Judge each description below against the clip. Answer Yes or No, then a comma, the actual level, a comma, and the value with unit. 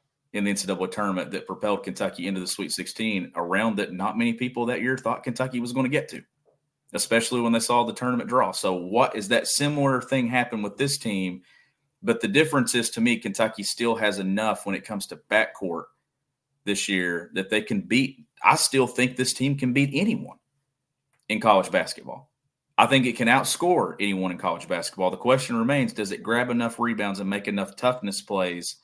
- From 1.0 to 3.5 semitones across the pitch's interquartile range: No, average, 4.3 semitones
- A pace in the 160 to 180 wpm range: No, average, 200 wpm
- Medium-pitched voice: No, low, 120 Hz